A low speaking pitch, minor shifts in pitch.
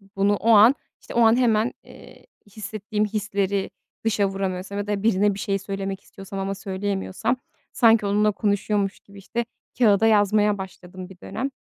No: high, 205 Hz; narrow, 1.6 semitones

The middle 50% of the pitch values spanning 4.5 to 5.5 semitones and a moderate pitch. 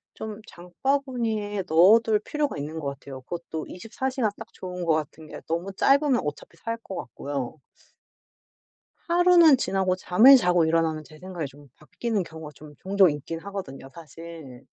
No: wide, 6.2 semitones; medium, 180 Hz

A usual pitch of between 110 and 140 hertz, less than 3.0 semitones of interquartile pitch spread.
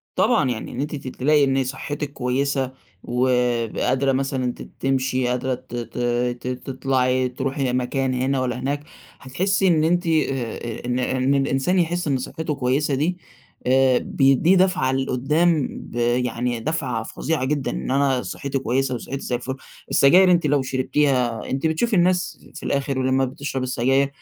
Yes: low, 135 Hz; narrow, 2.4 semitones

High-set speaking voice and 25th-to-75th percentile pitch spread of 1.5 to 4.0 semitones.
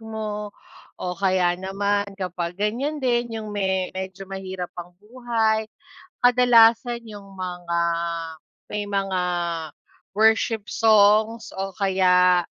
Yes: high, 205 Hz; average, 2.9 semitones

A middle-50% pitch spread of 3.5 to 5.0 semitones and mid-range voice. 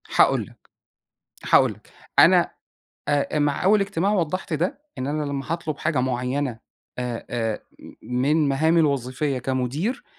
Yes: average, 4.1 semitones; medium, 145 Hz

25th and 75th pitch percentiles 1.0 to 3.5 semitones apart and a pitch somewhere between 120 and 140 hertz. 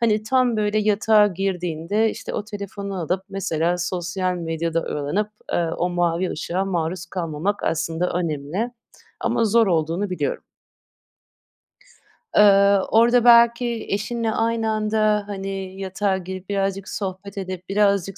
No: average, 3.1 semitones; high, 195 Hz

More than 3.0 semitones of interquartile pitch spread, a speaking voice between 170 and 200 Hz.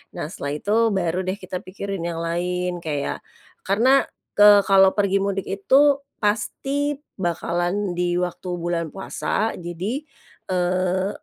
No: narrow, 2.6 semitones; medium, 185 Hz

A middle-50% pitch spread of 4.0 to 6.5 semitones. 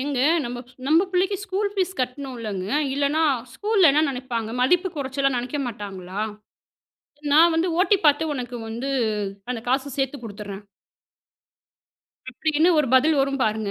Yes: average, 5.0 semitones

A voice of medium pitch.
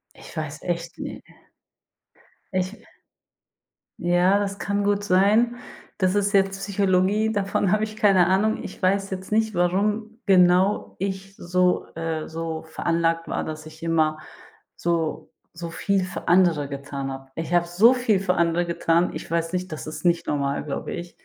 Yes: medium, 180 Hz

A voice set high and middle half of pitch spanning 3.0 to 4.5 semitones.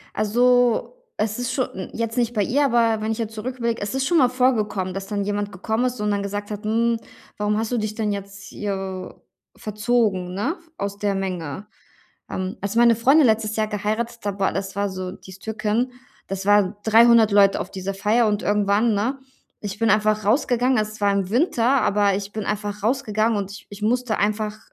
No: high, 215 Hz; narrow, 2.6 semitones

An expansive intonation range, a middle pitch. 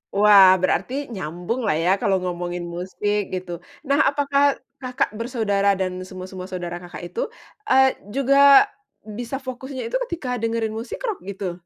No: wide, 5.7 semitones; high, 210 Hz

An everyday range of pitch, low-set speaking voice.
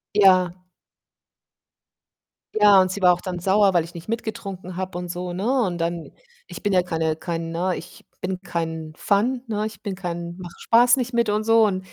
No: average, 3.2 semitones; medium, 185 Hz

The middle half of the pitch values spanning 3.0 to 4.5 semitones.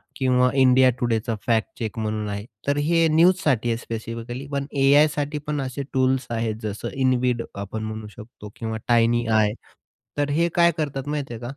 Yes: average, 4.1 semitones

